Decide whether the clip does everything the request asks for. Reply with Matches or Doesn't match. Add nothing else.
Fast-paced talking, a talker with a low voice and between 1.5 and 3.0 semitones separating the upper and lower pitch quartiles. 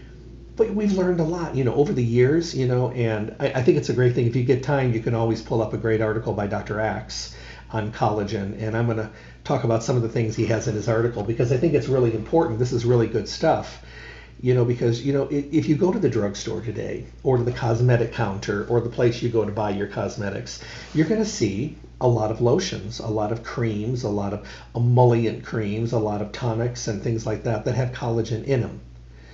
Matches